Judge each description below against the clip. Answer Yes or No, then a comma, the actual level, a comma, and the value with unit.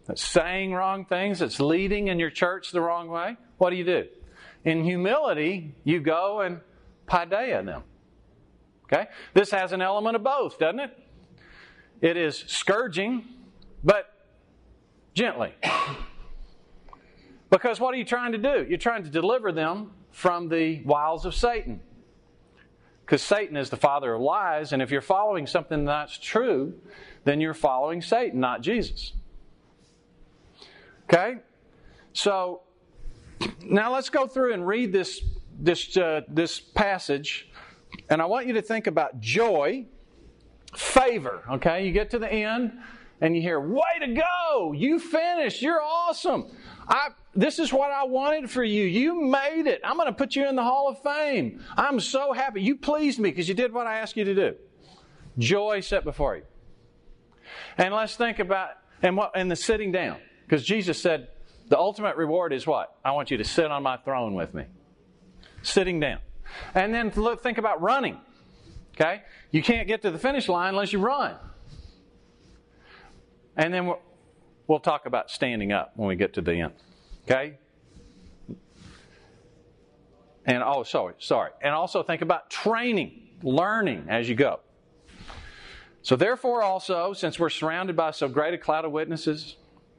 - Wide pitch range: Yes, wide, 6.8 semitones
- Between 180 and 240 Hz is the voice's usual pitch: Yes, high, 190 Hz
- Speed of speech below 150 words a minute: No, average, 160 wpm